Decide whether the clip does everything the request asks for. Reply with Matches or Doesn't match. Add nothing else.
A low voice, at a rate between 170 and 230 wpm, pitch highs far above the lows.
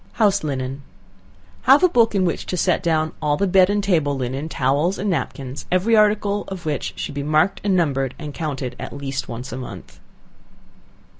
Doesn't match